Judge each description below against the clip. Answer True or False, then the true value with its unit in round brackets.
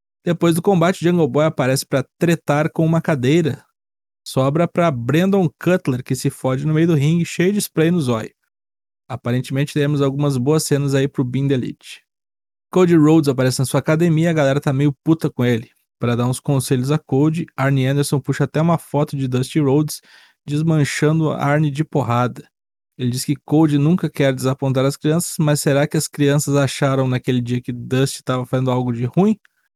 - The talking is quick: True (190 wpm)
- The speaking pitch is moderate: True (145 Hz)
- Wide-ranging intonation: False (3.2 semitones)